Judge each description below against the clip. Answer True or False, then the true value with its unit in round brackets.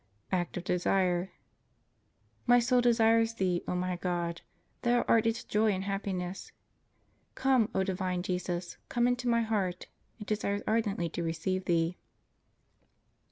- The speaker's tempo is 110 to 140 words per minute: True (135 wpm)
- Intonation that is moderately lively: True (4.1 semitones)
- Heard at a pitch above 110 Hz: True (190 Hz)